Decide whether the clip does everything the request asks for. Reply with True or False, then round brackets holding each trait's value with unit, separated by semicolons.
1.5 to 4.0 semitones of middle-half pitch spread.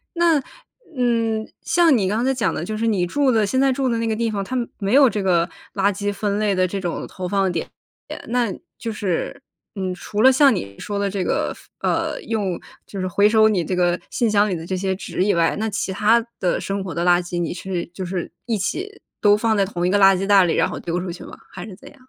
True (3.5 semitones)